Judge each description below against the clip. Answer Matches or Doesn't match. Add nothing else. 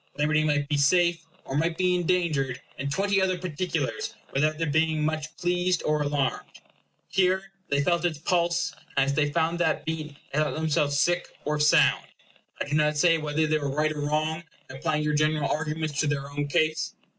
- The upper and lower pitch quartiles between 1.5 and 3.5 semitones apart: Matches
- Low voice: Doesn't match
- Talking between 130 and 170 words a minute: Doesn't match